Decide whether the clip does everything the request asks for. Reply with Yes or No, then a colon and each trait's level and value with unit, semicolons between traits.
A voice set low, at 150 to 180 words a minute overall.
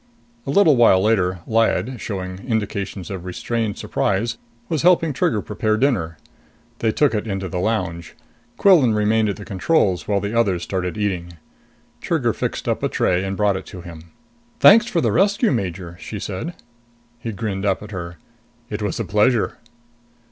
Yes: low, 105 Hz; average, 170 wpm